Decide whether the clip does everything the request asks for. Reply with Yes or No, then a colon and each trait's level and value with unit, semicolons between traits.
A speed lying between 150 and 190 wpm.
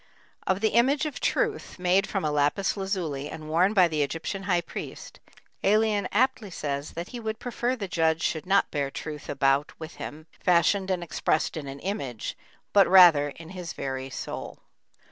Yes: average, 180 wpm